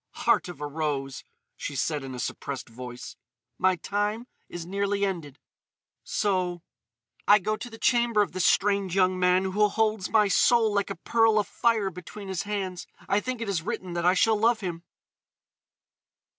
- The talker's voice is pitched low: No, high, 190 Hz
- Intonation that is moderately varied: Yes, average, 3.4 semitones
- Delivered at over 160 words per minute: Yes, average, 170 wpm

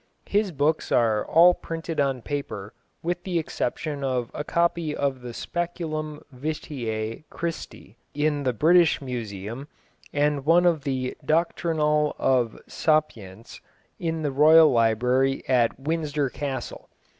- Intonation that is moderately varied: Yes, average, 4.3 semitones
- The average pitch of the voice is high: No, medium, 145 Hz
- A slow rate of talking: Yes, slow, 125 wpm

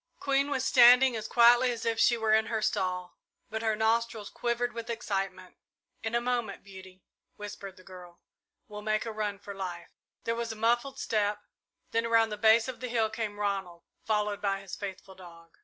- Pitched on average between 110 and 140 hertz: No, high, 220 Hz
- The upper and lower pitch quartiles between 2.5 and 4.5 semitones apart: Yes, average, 2.9 semitones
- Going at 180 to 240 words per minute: Yes, average, 190 wpm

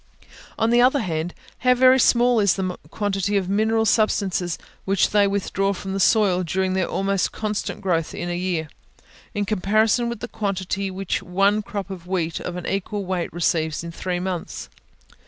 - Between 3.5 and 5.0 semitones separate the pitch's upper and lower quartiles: No, average, 2.8 semitones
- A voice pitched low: No, high, 195 Hz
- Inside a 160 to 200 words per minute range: Yes, average, 175 wpm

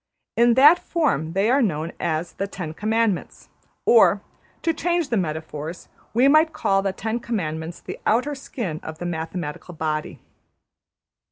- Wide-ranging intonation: Yes, wide, 7.7 semitones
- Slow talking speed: No, average, 150 wpm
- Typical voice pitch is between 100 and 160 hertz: No, high, 195 Hz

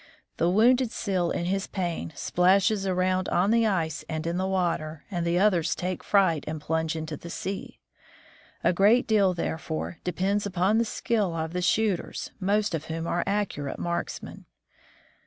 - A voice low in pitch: No, medium, 180 Hz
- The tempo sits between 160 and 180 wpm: Yes, average, 165 wpm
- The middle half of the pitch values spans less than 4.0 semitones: Yes, average, 3.2 semitones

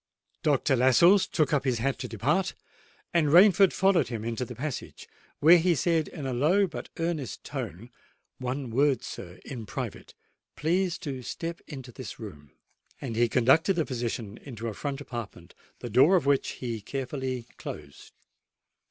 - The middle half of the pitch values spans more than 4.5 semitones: Yes, wide, 5.4 semitones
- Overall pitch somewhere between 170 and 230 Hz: No, low, 135 Hz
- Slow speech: No, average, 160 wpm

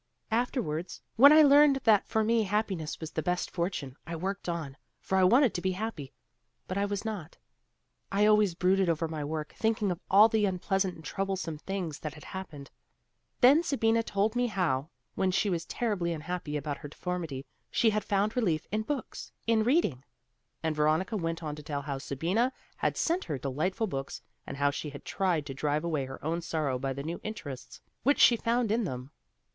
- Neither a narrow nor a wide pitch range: No, wide, 6.1 semitones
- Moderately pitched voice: Yes, medium, 180 Hz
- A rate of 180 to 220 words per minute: Yes, average, 195 wpm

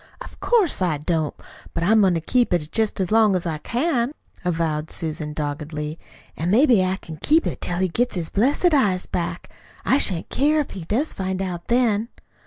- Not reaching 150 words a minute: No, average, 195 wpm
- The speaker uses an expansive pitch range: Yes, wide, 6.6 semitones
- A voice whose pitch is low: No, medium, 185 Hz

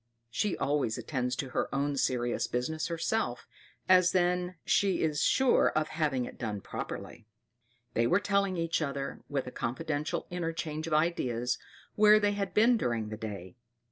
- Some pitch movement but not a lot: No, wide, 6.5 semitones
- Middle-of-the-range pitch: Yes, medium, 155 Hz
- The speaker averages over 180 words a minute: No, average, 160 wpm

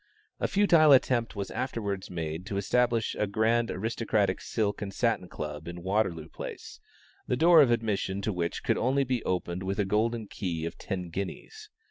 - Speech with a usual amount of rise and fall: Yes, average, 4.2 semitones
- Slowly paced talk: No, average, 175 wpm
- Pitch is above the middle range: No, low, 105 Hz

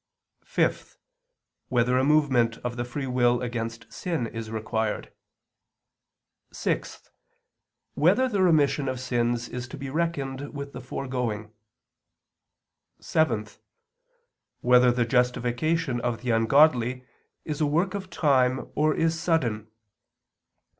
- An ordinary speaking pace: No, slow, 115 wpm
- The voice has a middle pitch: No, low, 125 Hz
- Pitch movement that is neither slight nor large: Yes, average, 4.0 semitones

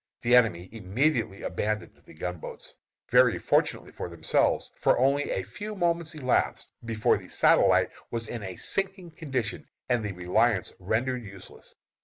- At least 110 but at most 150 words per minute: Yes, average, 145 wpm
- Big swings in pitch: Yes, wide, 6.0 semitones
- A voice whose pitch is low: Yes, low, 115 Hz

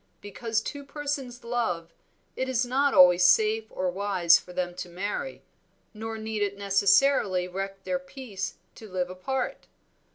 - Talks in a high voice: Yes, high, 205 Hz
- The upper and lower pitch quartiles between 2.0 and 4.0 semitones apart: No, average, 5.3 semitones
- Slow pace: No, average, 150 wpm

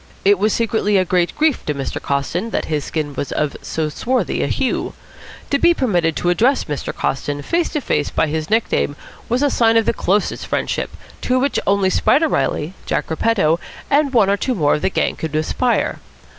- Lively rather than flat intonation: Yes, wide, 7.8 semitones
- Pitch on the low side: No, high, 195 Hz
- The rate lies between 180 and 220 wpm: Yes, average, 200 wpm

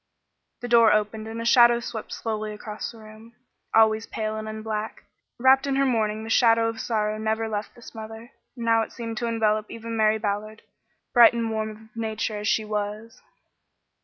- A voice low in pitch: No, high, 220 Hz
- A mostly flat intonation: Yes, narrow, 1.1 semitones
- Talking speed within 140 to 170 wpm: No, average, 190 wpm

